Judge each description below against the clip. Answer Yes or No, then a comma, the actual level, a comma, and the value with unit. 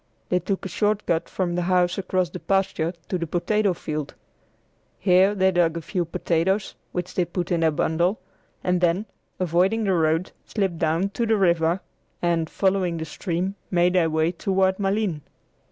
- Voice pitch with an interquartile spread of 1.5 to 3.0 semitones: Yes, narrow, 2.4 semitones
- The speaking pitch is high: No, medium, 180 Hz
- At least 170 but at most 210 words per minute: Yes, average, 175 wpm